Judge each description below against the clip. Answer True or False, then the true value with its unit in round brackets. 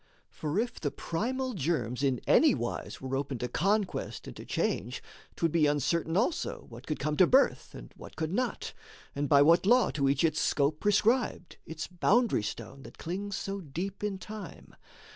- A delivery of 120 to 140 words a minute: False (180 wpm)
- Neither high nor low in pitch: True (165 Hz)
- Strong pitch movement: True (6.3 semitones)